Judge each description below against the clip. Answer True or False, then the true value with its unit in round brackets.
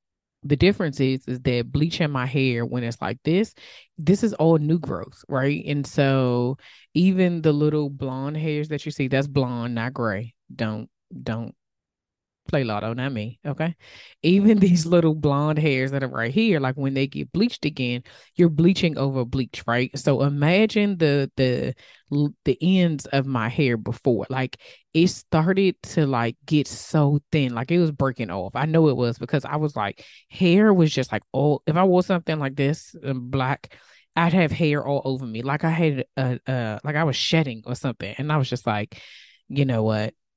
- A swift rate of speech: False (190 wpm)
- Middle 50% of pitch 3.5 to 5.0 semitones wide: True (4.2 semitones)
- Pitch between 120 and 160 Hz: True (140 Hz)